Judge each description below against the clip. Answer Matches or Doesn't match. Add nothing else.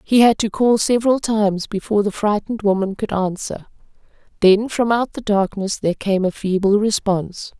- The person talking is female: Matches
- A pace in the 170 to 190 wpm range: Matches